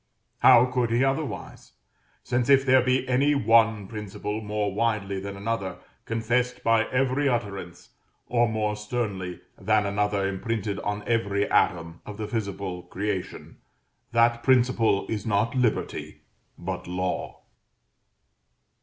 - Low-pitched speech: Yes, low, 110 Hz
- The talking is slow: Yes, slow, 125 wpm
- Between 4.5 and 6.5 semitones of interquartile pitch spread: No, average, 3.3 semitones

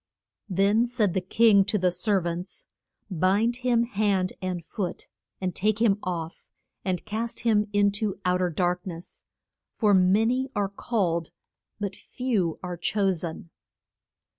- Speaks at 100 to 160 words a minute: Yes, average, 150 wpm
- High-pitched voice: Yes, high, 195 Hz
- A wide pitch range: No, average, 3.2 semitones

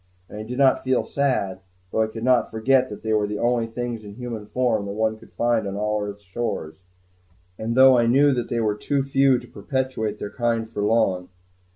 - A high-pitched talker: No, low, 115 Hz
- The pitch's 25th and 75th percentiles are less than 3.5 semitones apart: Yes, average, 3.1 semitones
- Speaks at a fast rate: Yes, fast, 220 wpm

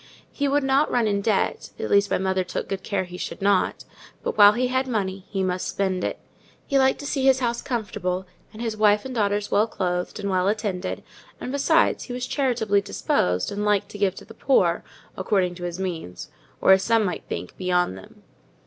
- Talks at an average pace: No, fast, 210 wpm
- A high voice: Yes, high, 200 Hz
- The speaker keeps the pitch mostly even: No, average, 4.1 semitones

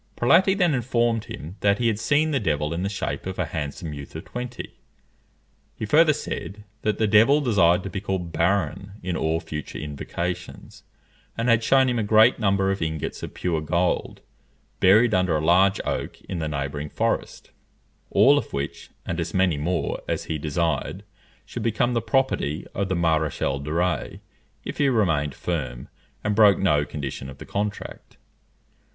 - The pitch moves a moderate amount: No, wide, 6.0 semitones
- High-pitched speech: No, very low, 95 Hz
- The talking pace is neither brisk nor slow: Yes, average, 175 wpm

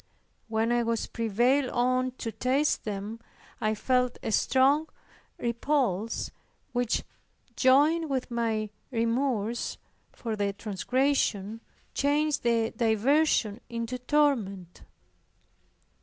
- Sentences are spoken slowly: Yes, slow, 95 wpm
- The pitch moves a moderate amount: Yes, average, 3.3 semitones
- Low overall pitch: No, high, 235 Hz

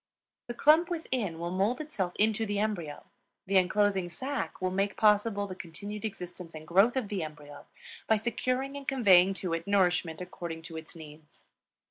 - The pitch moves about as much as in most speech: Yes, average, 4.3 semitones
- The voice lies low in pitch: No, high, 195 Hz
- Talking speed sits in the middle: Yes, average, 170 wpm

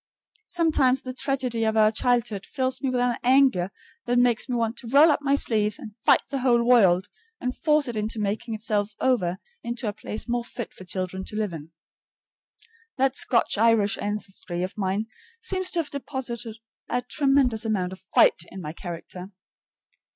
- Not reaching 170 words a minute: No, average, 180 wpm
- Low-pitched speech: No, high, 235 Hz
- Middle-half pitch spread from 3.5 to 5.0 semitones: Yes, average, 3.9 semitones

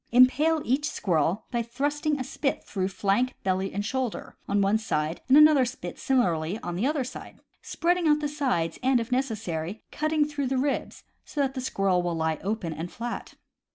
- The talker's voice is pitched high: Yes, high, 240 Hz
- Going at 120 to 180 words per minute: No, average, 190 wpm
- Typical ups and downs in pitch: No, wide, 6.9 semitones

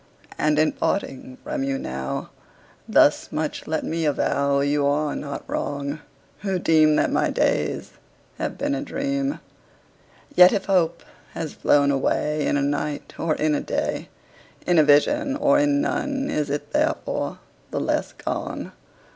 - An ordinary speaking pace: Yes, average, 155 wpm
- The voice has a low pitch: No, medium, 155 Hz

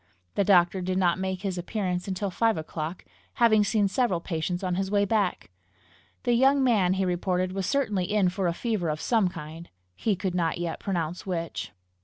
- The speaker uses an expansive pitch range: No, average, 2.8 semitones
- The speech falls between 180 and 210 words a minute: Yes, average, 190 wpm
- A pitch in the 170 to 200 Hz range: Yes, medium, 185 Hz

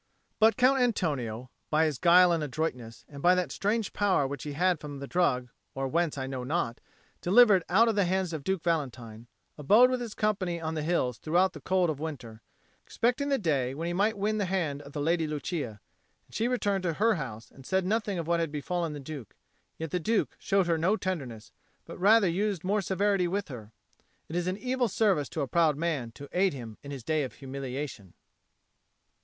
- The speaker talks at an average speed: No, fast, 215 wpm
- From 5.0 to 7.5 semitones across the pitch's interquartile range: Yes, wide, 5.6 semitones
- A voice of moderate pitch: Yes, medium, 170 Hz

